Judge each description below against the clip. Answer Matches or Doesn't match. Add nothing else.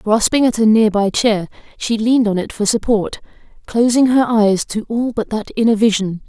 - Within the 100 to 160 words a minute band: Doesn't match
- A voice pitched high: Matches